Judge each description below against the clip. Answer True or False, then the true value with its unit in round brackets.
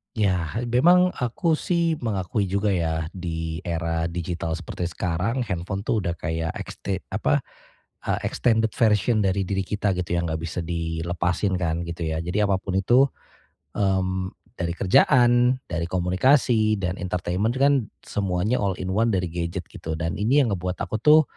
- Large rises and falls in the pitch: False (4.3 semitones)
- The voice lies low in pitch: True (95 Hz)